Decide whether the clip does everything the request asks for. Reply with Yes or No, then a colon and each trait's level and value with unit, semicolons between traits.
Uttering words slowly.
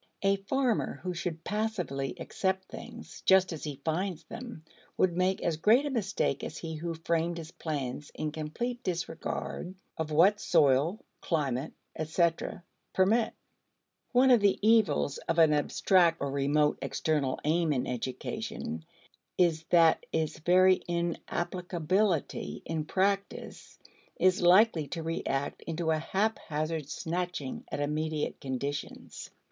Yes: slow, 130 wpm